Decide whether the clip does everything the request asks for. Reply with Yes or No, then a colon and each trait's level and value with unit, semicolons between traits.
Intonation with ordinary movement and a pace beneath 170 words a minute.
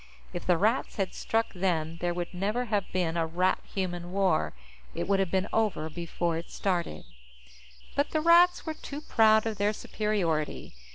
No: average, 4.1 semitones; average, 175 wpm